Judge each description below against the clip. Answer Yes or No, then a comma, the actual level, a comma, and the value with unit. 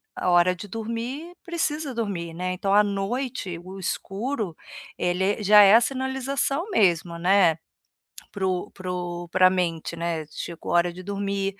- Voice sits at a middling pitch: No, high, 195 Hz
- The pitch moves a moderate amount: Yes, average, 4.5 semitones